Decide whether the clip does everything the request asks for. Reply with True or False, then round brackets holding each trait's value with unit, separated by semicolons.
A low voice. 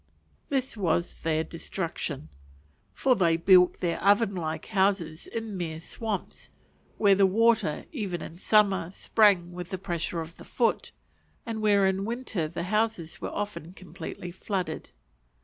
False (190 Hz)